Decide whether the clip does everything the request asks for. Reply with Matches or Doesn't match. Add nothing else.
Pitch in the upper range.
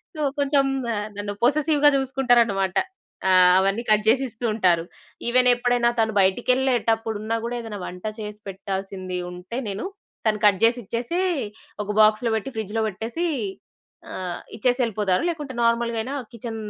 Matches